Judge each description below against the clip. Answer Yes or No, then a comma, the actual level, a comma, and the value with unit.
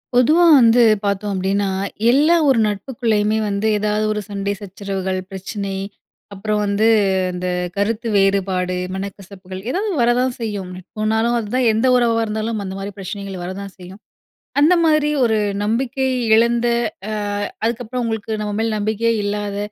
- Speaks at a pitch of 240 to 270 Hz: No, high, 210 Hz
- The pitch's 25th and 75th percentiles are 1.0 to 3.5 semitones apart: Yes, average, 2.8 semitones